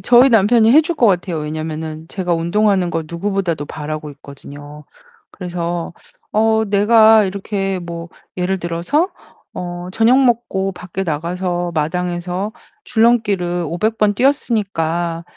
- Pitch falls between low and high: Yes, medium, 180 Hz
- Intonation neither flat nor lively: Yes, average, 4.3 semitones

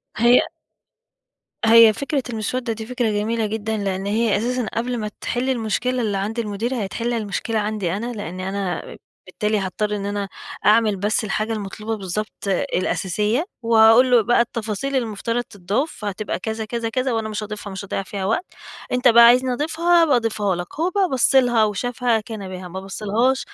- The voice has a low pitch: No, high, 220 Hz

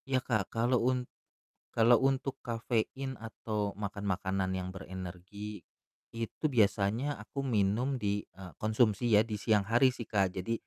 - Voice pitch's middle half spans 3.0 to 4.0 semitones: Yes, average, 3.6 semitones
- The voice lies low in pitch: Yes, low, 110 Hz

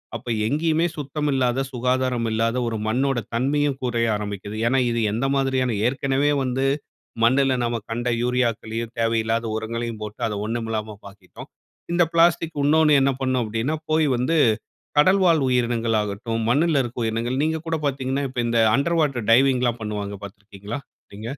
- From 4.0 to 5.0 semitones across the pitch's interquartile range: No, average, 3.4 semitones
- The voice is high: No, low, 125 Hz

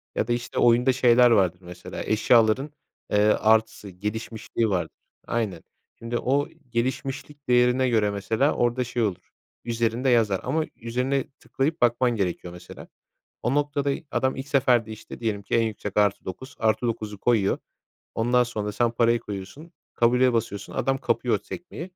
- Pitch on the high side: No, low, 115 Hz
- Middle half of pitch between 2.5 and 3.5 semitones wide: Yes, average, 3.2 semitones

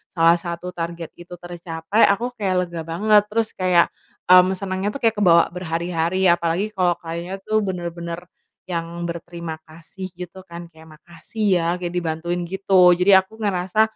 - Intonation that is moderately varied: No, narrow, 2.1 semitones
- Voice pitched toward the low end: No, medium, 175 Hz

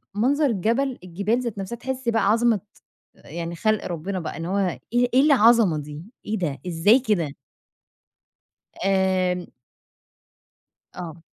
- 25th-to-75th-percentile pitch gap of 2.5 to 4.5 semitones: No, wide, 5.5 semitones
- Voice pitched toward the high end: Yes, high, 200 Hz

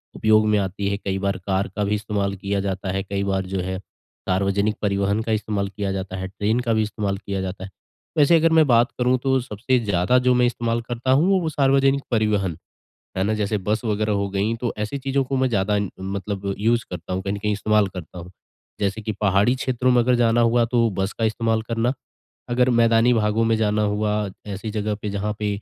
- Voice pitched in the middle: No, low, 105 Hz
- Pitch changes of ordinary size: Yes, average, 3.1 semitones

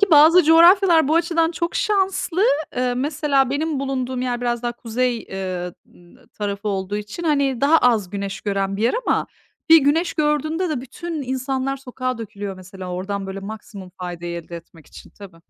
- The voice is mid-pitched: No, very high, 250 Hz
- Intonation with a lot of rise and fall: Yes, wide, 7.5 semitones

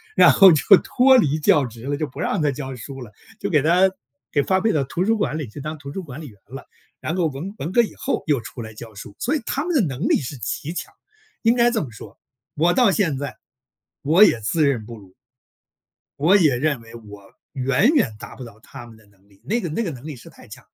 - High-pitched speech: No, medium, 145 Hz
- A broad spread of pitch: Yes, wide, 6.9 semitones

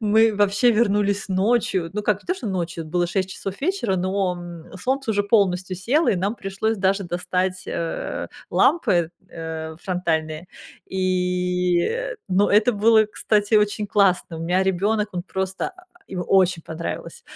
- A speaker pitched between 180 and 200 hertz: Yes, high, 190 Hz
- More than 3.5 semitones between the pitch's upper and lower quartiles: No, average, 2.8 semitones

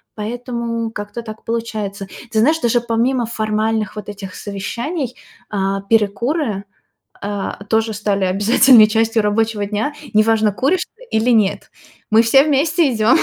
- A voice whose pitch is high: Yes, high, 225 Hz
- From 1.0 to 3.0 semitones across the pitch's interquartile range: Yes, narrow, 2.4 semitones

